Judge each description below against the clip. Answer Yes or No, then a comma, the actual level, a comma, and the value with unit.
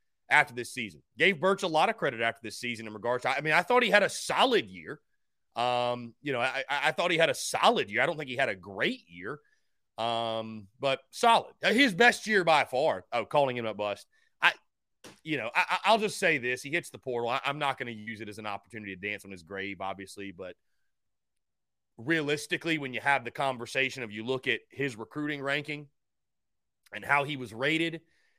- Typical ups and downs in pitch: No, wide, 6.3 semitones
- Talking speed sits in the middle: No, fast, 220 wpm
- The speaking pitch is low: Yes, low, 130 Hz